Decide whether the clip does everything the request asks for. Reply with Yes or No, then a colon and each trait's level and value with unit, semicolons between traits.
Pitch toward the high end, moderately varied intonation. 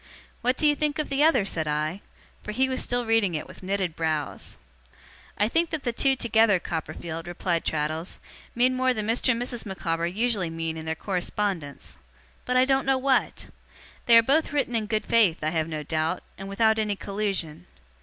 No: high, 210 Hz; wide, 7.2 semitones